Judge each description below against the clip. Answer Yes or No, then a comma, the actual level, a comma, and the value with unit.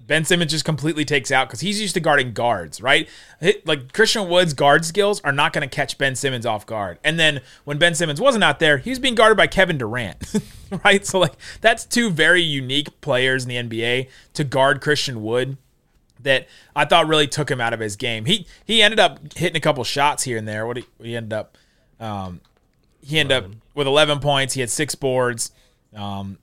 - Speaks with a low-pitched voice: No, medium, 145 Hz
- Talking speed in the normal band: No, fast, 220 wpm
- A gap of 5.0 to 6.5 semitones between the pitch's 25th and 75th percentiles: Yes, wide, 5.4 semitones